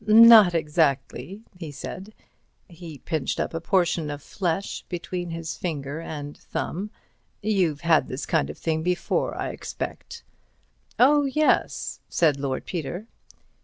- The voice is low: No, medium, 170 Hz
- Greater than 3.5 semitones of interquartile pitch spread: Yes, average, 4.3 semitones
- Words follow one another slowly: Yes, slow, 130 wpm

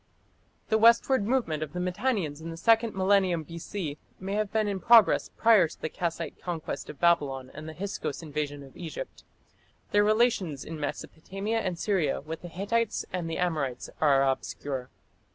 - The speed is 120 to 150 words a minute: No, average, 170 wpm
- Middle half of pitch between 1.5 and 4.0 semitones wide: No, average, 5.2 semitones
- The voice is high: No, medium, 175 Hz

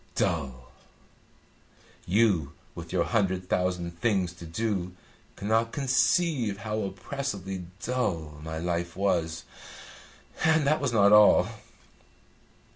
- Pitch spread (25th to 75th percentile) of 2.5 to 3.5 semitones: No, average, 4.9 semitones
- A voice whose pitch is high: No, very low, 95 Hz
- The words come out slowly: Yes, slow, 105 wpm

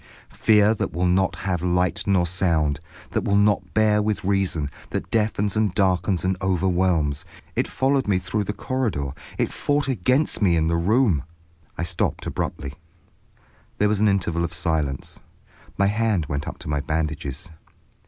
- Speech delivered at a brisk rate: No, average, 165 wpm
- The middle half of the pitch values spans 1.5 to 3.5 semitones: No, average, 3.9 semitones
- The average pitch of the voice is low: Yes, very low, 95 Hz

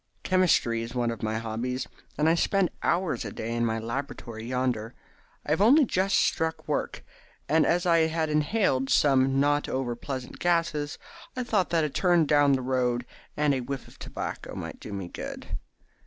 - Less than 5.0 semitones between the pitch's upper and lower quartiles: No, wide, 5.5 semitones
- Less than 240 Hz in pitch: Yes, medium, 140 Hz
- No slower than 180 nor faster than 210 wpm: Yes, average, 185 wpm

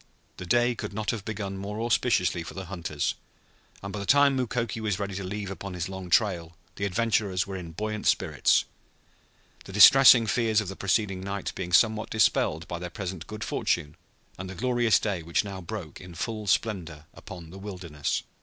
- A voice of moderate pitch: No, low, 100 Hz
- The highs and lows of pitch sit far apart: No, average, 3.3 semitones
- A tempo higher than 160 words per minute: Yes, average, 190 wpm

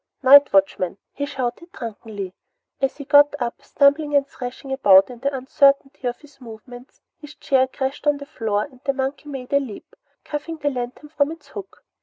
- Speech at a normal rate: Yes, average, 185 wpm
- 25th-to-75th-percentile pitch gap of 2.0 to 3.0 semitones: Yes, average, 2.7 semitones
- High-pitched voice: Yes, very high, 270 Hz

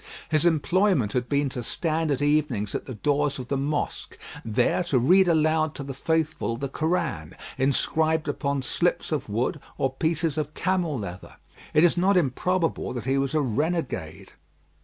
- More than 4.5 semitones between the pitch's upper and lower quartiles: No, average, 3.9 semitones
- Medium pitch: Yes, medium, 145 Hz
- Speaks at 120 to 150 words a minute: No, average, 170 wpm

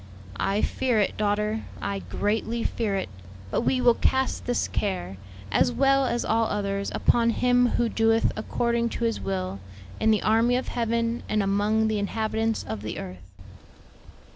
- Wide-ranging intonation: No, average, 3.0 semitones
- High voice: Yes, high, 220 Hz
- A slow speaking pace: No, average, 165 wpm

